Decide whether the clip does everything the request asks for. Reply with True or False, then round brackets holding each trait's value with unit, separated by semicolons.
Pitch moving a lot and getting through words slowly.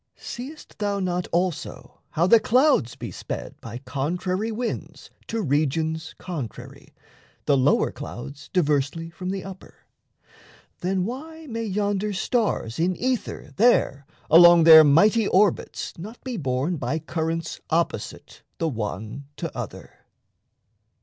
True (6.1 semitones; 125 wpm)